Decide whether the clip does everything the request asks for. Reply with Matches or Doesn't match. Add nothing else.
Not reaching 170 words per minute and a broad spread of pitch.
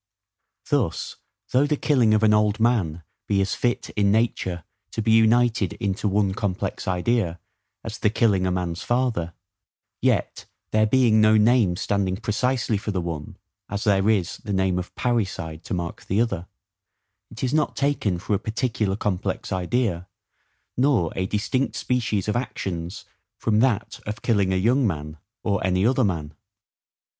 Doesn't match